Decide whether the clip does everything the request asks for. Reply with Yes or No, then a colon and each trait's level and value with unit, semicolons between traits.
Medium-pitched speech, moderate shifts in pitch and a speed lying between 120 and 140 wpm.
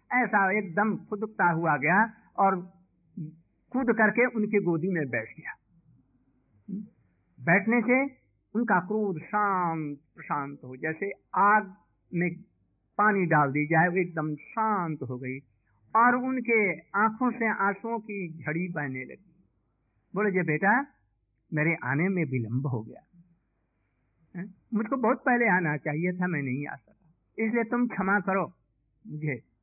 No: medium, 175 Hz; wide, 6.4 semitones; average, 130 wpm